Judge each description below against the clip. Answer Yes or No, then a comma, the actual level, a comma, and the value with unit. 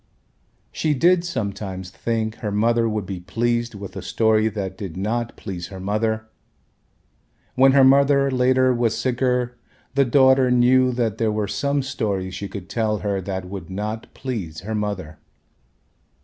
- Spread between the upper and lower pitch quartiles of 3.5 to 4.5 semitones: Yes, average, 4.1 semitones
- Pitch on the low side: Yes, low, 110 Hz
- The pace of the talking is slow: No, average, 155 wpm